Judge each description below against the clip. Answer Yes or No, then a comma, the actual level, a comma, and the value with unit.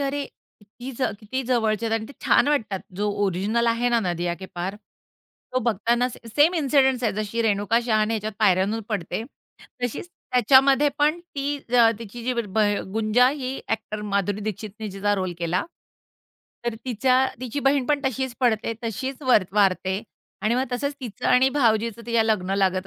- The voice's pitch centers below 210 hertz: No, high, 230 Hz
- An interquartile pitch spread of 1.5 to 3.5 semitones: No, average, 4.0 semitones